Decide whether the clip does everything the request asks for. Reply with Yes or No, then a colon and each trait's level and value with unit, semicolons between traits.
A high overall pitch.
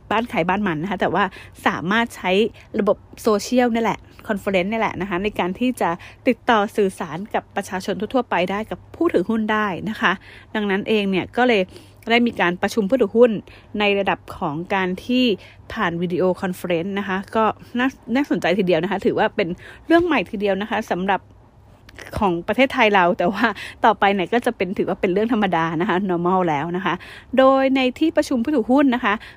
Yes: high, 205 Hz